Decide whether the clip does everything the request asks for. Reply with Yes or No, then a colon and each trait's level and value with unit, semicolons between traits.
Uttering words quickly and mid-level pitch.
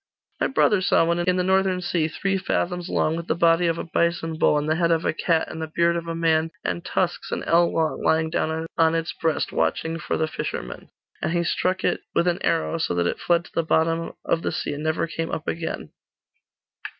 Yes: fast, 235 wpm; medium, 165 Hz